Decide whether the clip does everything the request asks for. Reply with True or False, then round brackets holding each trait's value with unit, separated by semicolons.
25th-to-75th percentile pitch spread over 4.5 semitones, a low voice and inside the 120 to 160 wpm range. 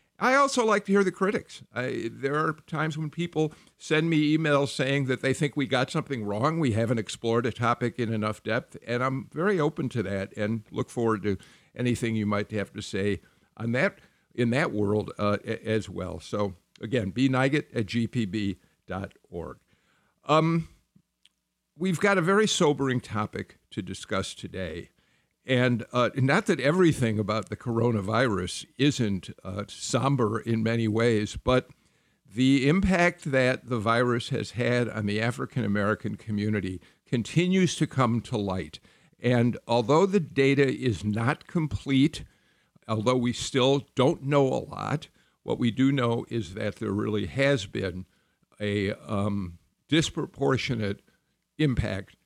True (5.0 semitones; 120 Hz; 150 wpm)